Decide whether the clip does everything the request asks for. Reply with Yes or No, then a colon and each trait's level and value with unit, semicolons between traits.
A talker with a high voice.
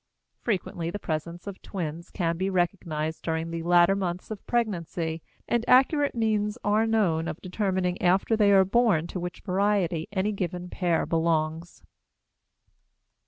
No: medium, 180 Hz